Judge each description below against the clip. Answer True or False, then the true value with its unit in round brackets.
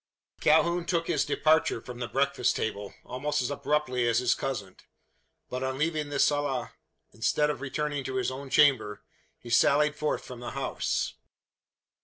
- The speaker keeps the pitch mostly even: False (3.0 semitones)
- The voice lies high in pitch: False (135 Hz)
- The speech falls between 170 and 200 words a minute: False (160 wpm)